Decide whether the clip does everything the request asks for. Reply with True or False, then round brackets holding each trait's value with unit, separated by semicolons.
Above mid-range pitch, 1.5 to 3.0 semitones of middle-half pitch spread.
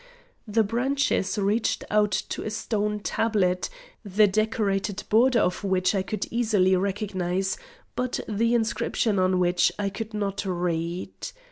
True (205 Hz; 2.7 semitones)